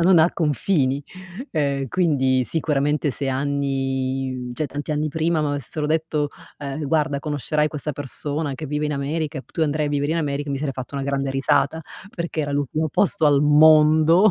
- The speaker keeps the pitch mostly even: Yes, narrow, 2.0 semitones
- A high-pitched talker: No, medium, 145 Hz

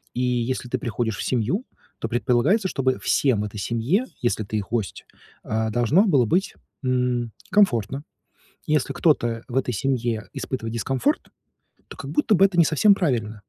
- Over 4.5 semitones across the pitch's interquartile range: Yes, average, 5.0 semitones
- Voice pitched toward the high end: No, low, 125 Hz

